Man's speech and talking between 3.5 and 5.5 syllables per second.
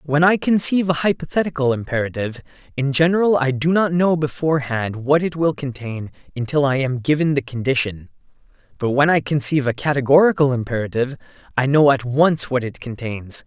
No: male; 5.8 syllables/s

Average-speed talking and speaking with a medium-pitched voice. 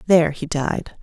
Yes: average, 175 wpm; medium, 160 Hz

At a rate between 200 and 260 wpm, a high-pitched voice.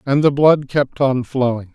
No: fast, 205 wpm; low, 130 Hz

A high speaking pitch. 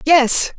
Yes: very high, 290 Hz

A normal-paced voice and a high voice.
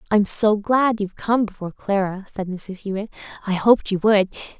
Yes: average, 185 wpm; high, 205 Hz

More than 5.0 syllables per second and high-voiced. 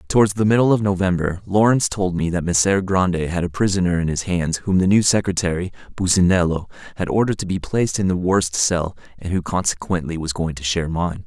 No: 6.0 syllables/s; very low, 90 Hz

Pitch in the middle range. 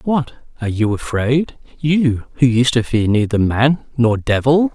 No: low, 125 Hz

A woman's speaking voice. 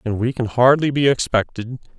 No: male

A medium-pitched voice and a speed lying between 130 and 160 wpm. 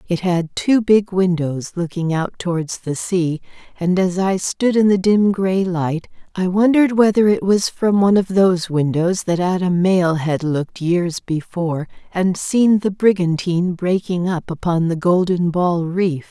No: medium, 180 Hz; average, 175 wpm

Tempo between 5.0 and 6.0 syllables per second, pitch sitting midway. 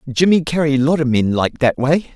Yes: 5.1 syllables/s; medium, 145 Hz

